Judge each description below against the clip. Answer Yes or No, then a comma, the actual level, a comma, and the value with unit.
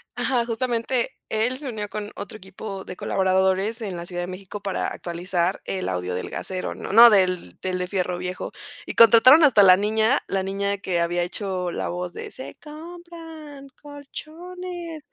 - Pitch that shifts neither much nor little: No, wide, 6.1 semitones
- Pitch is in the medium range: No, high, 205 Hz